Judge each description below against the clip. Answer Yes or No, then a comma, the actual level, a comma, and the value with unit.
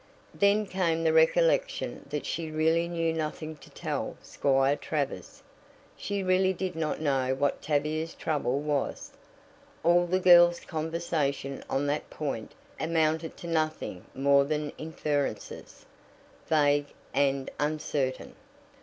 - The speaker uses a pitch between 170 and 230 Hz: No, medium, 155 Hz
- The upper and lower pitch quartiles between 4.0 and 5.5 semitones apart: No, average, 2.8 semitones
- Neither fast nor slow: No, slow, 120 wpm